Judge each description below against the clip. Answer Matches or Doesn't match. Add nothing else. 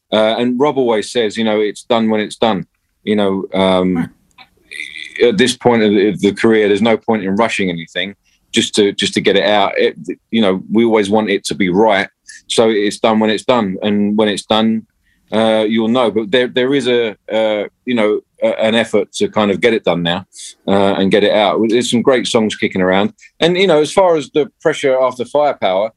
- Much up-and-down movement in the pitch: Doesn't match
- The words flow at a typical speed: Doesn't match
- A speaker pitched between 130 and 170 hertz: Doesn't match